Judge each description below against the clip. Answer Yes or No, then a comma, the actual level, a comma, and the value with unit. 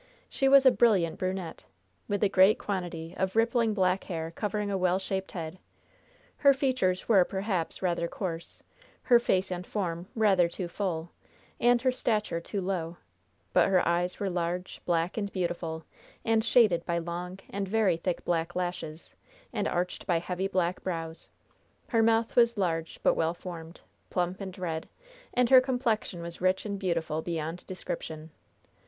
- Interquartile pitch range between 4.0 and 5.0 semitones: No, average, 3.4 semitones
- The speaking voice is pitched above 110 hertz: Yes, medium, 185 Hz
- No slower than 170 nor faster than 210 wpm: No, average, 160 wpm